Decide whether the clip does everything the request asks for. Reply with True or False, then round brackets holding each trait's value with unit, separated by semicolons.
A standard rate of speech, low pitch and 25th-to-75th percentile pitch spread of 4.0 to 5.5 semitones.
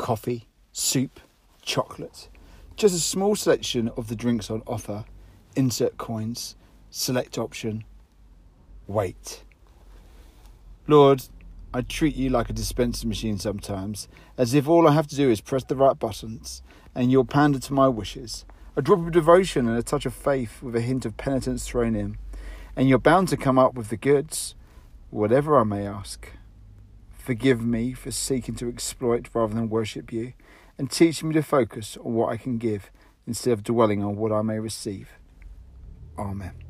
True (165 wpm; 115 Hz; 4.4 semitones)